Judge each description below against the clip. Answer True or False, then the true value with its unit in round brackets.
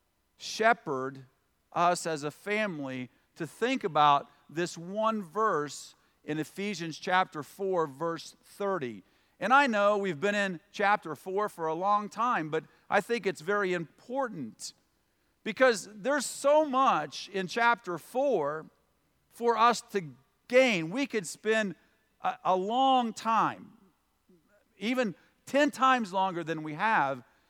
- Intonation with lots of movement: True (6.2 semitones)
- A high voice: True (200 Hz)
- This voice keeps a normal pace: False (130 wpm)